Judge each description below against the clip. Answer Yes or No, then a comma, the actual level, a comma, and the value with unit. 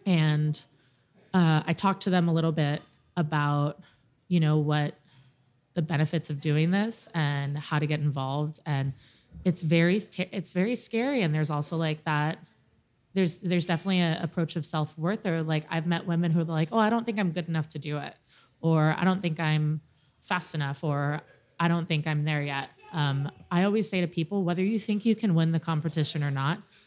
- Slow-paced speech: No, average, 200 wpm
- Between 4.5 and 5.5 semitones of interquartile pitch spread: No, average, 3.1 semitones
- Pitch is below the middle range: No, medium, 160 Hz